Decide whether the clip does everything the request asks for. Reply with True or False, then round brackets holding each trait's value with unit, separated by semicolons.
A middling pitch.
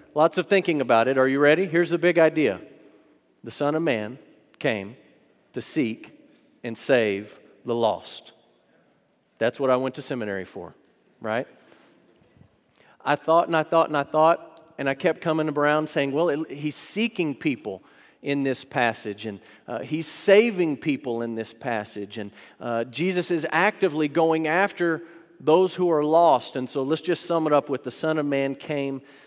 True (150 Hz)